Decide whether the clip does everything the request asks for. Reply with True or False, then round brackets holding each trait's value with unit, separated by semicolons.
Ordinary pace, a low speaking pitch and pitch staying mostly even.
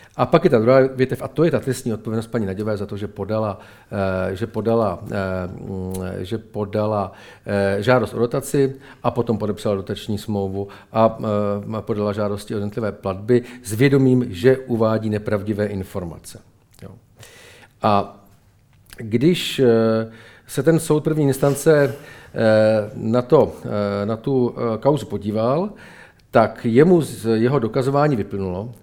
False (125 wpm; 110 Hz; 3.6 semitones)